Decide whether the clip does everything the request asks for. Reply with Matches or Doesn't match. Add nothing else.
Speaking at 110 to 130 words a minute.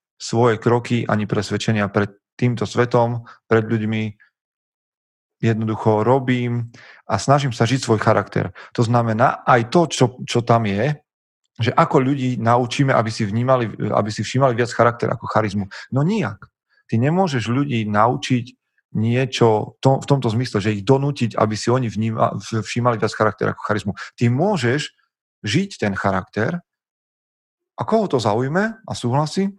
Doesn't match